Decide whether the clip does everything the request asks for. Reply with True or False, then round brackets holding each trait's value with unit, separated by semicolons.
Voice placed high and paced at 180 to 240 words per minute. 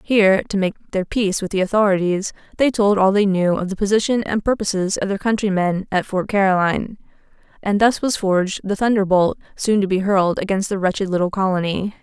True (195 Hz; 195 wpm)